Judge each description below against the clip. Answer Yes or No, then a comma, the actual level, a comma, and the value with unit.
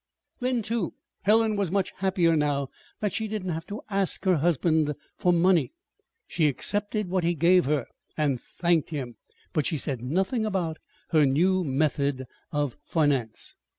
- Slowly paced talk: No, average, 160 wpm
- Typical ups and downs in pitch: Yes, average, 4.6 semitones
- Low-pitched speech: No, medium, 170 Hz